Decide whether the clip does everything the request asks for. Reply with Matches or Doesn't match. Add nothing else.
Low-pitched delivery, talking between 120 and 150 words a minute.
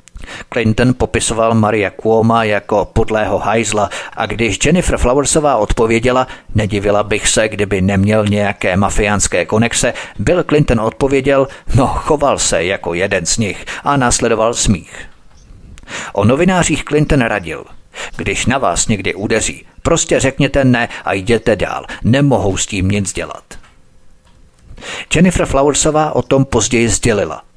Matches